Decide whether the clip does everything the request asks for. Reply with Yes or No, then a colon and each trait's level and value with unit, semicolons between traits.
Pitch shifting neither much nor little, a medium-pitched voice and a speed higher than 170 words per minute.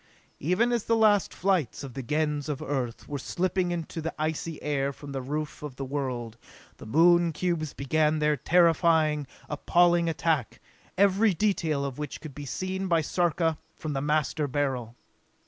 No: average, 3.6 semitones; medium, 155 Hz; average, 165 wpm